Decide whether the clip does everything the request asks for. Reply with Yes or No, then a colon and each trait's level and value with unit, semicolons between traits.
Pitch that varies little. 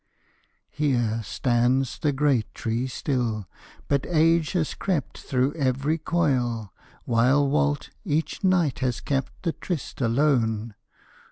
No: average, 4.1 semitones